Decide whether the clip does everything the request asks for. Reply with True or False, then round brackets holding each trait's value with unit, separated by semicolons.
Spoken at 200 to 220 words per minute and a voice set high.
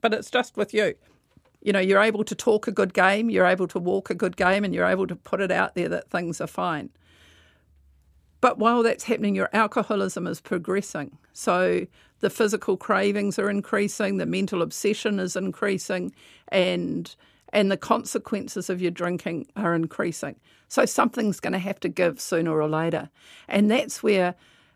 False (180 wpm; 195 Hz)